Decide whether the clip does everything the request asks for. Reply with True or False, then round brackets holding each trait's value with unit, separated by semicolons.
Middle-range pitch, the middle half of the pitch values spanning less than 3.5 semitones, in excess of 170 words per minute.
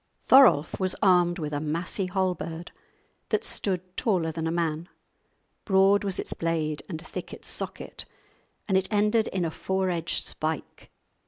False (180 Hz; 2.9 semitones; 155 wpm)